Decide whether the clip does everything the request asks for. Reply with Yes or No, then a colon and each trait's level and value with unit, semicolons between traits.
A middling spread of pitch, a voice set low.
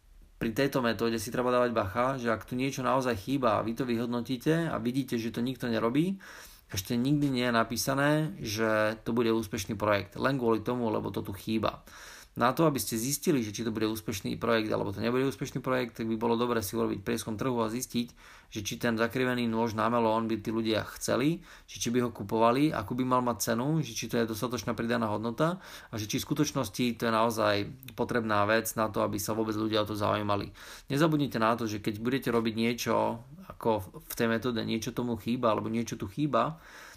No: narrow, 2.2 semitones; low, 115 Hz